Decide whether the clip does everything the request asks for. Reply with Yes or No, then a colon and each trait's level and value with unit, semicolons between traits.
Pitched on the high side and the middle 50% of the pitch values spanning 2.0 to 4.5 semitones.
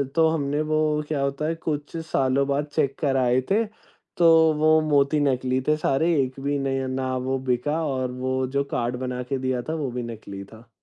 No: low, 135 Hz; average, 2.8 semitones